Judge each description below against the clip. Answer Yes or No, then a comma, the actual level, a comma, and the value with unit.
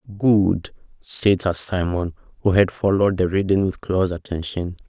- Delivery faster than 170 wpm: No, average, 150 wpm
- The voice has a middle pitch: No, very low, 95 Hz